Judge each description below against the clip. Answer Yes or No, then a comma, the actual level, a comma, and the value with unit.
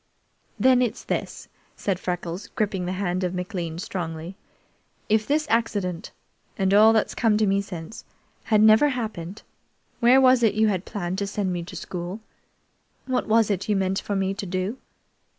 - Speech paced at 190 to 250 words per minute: No, average, 170 wpm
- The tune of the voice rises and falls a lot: No, average, 3.3 semitones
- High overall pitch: Yes, high, 200 Hz